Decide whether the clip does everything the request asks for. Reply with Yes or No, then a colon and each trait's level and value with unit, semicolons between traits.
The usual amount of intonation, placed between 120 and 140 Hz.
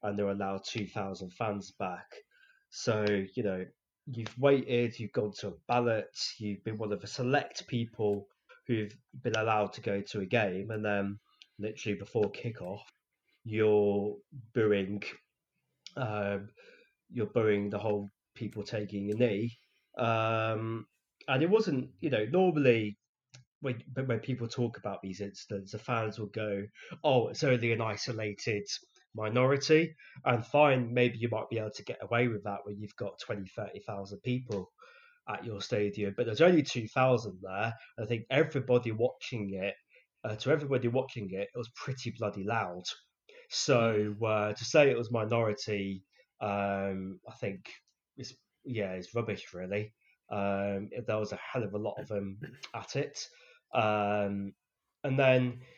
No: average, 3.5 semitones; low, 110 Hz